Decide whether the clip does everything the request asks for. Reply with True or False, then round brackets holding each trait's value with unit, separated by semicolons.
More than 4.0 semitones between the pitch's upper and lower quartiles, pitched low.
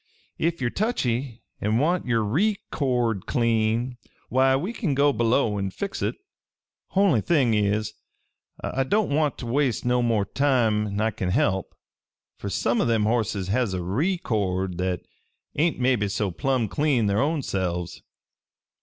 True (5.2 semitones; 120 Hz)